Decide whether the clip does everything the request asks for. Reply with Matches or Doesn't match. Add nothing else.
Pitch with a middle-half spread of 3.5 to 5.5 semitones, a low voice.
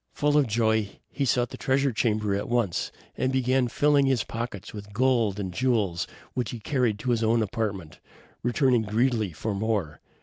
Matches